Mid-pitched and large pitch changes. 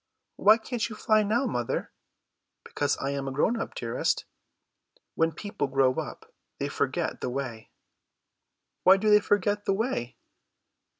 No: high, 195 Hz; wide, 8.0 semitones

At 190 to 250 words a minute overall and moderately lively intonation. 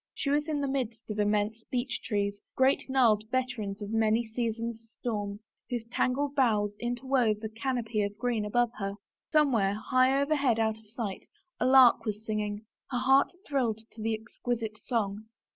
No: average, 170 wpm; average, 3.2 semitones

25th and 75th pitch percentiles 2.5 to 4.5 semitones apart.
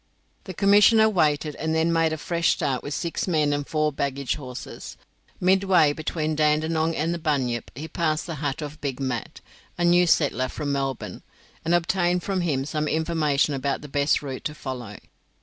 Yes: average, 3.1 semitones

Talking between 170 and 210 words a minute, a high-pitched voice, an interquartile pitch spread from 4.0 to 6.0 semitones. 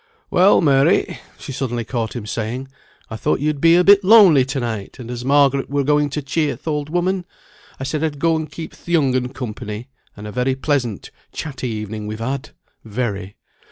No: average, 195 wpm; low, 135 Hz; average, 4.4 semitones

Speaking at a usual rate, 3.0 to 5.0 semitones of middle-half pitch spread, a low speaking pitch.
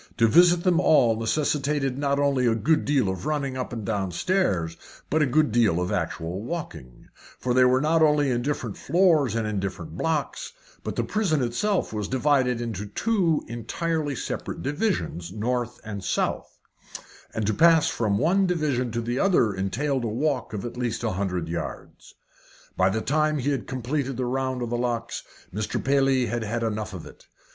No: average, 185 wpm; wide, 5.4 semitones; low, 125 Hz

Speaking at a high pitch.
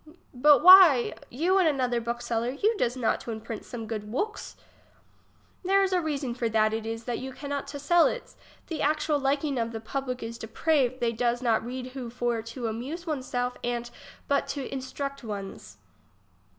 Yes: very high, 250 Hz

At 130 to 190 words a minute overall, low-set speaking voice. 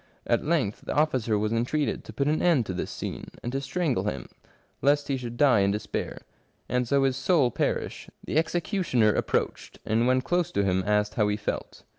No: average, 200 wpm; low, 125 Hz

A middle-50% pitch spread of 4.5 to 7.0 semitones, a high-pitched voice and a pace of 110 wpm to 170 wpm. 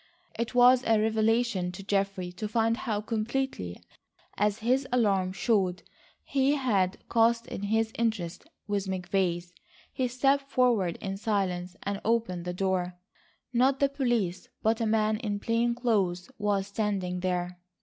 No: average, 4.0 semitones; high, 210 Hz; average, 145 wpm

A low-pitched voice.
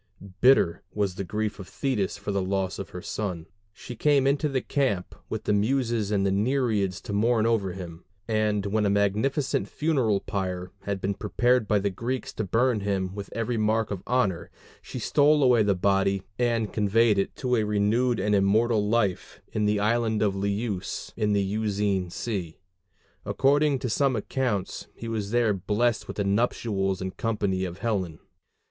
Yes: low, 105 Hz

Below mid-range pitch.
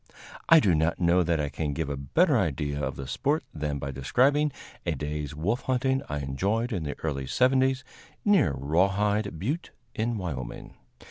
Yes: very low, 85 Hz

